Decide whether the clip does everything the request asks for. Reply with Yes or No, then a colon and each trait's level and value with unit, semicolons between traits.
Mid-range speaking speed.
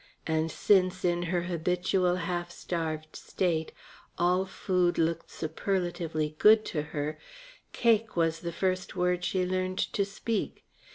No: slow, 130 wpm